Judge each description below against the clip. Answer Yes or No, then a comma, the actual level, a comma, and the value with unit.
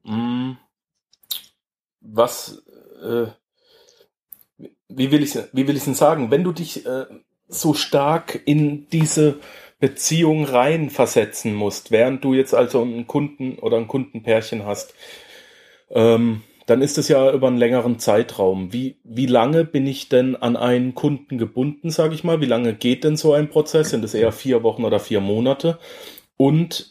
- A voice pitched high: No, low, 135 Hz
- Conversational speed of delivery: Yes, average, 155 wpm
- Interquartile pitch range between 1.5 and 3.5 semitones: No, average, 3.9 semitones